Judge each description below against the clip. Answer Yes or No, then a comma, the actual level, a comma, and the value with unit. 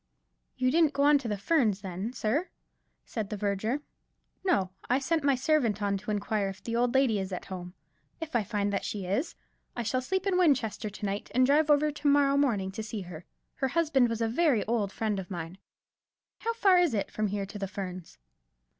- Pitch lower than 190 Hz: No, high, 225 Hz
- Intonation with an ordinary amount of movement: No, wide, 6.0 semitones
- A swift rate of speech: Yes, fast, 215 wpm